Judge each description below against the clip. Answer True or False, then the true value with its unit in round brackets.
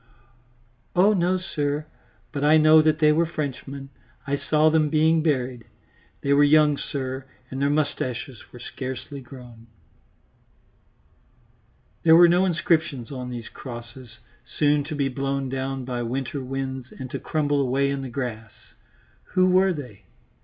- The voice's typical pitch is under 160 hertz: True (140 Hz)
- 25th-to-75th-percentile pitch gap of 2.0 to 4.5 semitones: True (3.1 semitones)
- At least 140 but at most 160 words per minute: True (145 wpm)